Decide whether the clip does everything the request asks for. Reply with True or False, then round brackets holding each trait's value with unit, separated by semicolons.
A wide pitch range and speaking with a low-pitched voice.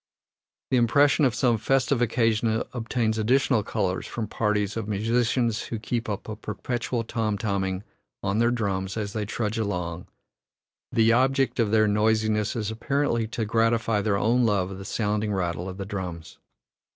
False (2.5 semitones; 110 Hz)